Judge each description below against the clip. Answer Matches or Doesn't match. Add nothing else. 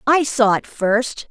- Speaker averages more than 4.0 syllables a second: Doesn't match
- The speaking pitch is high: Matches